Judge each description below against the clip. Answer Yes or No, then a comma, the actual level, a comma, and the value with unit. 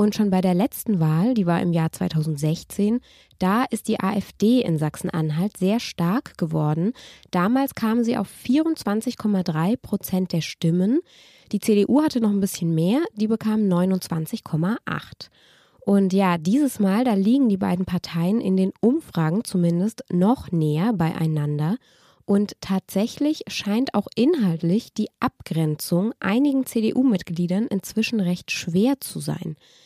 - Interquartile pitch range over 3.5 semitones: Yes, average, 4.5 semitones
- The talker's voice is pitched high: Yes, high, 200 Hz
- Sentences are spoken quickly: No, average, 135 wpm